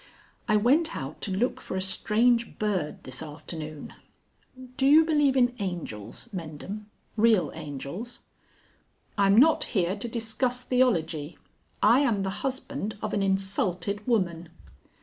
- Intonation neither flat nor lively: No, wide, 6.2 semitones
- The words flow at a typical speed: No, slow, 130 wpm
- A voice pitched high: Yes, high, 205 Hz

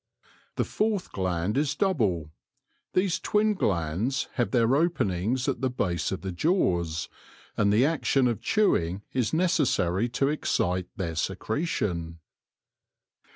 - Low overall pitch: Yes, low, 115 Hz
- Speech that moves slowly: Yes, slow, 125 wpm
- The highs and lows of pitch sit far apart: Yes, wide, 8.9 semitones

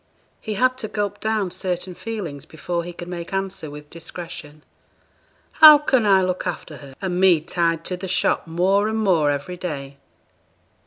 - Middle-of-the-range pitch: Yes, medium, 180 Hz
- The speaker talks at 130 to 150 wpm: No, average, 170 wpm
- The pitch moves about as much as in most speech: Yes, average, 3.3 semitones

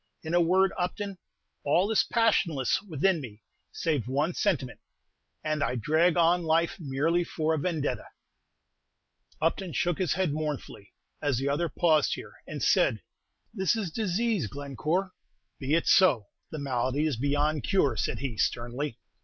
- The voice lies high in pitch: No, medium, 155 Hz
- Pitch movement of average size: Yes, average, 4.2 semitones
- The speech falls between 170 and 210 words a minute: No, average, 150 wpm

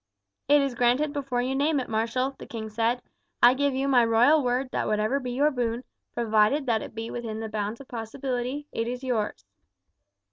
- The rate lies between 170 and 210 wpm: Yes, average, 200 wpm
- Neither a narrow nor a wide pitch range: Yes, average, 3.1 semitones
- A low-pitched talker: No, high, 245 Hz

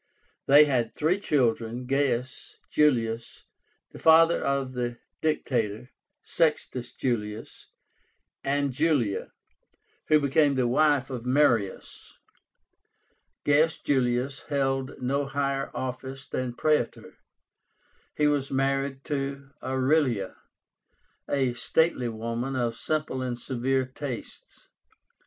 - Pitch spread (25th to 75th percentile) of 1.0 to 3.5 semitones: Yes, average, 2.8 semitones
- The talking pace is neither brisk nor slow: No, slow, 100 wpm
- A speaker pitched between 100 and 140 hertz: Yes, low, 135 Hz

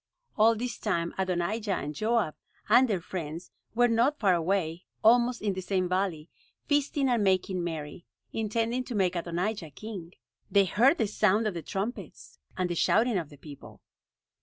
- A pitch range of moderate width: Yes, average, 4.6 semitones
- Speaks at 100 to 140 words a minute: No, average, 165 wpm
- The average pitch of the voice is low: No, high, 195 Hz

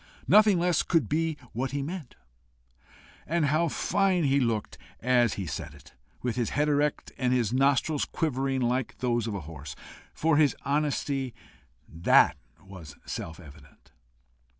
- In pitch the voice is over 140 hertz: No, low, 135 Hz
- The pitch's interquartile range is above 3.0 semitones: Yes, average, 4.9 semitones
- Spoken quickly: No, average, 150 wpm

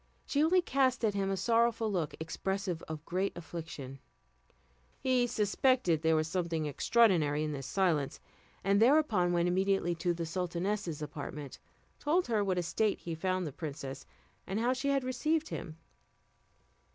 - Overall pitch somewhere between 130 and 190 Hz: Yes, medium, 185 Hz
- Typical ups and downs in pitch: No, wide, 6.1 semitones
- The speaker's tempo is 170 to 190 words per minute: No, average, 160 wpm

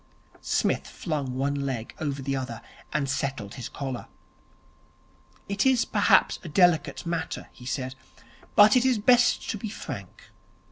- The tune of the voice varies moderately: No, wide, 7.3 semitones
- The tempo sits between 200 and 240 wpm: No, average, 145 wpm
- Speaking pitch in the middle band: Yes, medium, 145 Hz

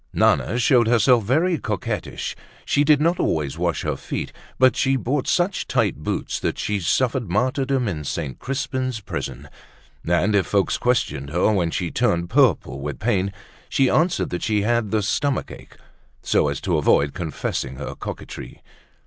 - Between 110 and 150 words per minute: No, average, 165 wpm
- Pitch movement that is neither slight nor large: No, wide, 6.9 semitones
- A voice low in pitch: Yes, low, 110 Hz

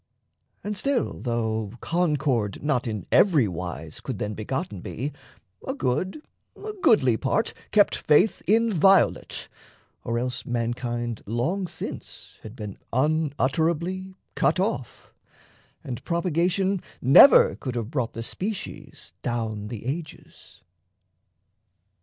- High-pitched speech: No, low, 135 Hz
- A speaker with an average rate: No, slow, 110 wpm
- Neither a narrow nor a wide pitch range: No, wide, 7.8 semitones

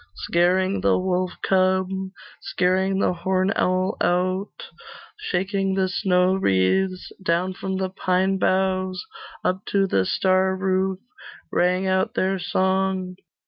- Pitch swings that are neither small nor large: No, narrow, 0.7 semitones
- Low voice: No, medium, 185 Hz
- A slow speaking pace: Yes, slow, 120 wpm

